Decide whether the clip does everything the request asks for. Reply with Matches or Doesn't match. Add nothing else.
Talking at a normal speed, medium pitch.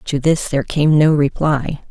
Matches